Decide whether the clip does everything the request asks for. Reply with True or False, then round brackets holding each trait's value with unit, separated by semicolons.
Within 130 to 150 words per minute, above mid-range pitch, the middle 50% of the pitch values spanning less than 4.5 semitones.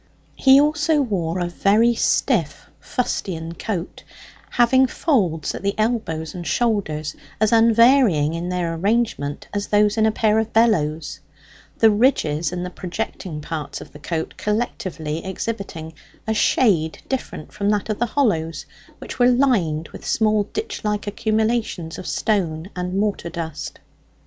False (145 wpm; 200 Hz; 5.6 semitones)